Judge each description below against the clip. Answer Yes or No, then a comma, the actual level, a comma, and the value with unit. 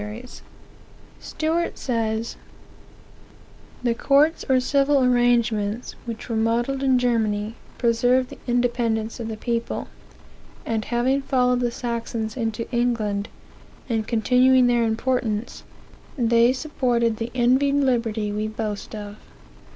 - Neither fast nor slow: No, slow, 110 wpm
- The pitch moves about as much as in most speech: No, narrow, 2.2 semitones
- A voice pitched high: Yes, high, 235 Hz